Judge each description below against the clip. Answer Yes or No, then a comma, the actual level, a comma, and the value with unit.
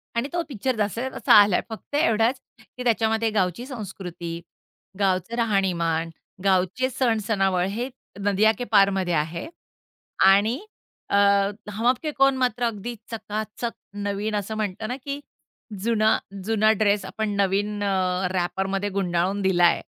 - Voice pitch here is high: Yes, high, 205 Hz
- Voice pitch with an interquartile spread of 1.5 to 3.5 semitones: Yes, average, 3.2 semitones